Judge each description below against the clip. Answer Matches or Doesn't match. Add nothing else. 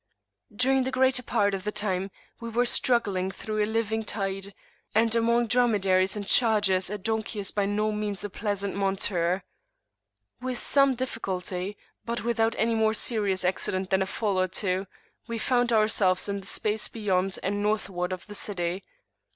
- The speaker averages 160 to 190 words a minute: Matches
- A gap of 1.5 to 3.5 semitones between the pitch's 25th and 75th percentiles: Matches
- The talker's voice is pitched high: Matches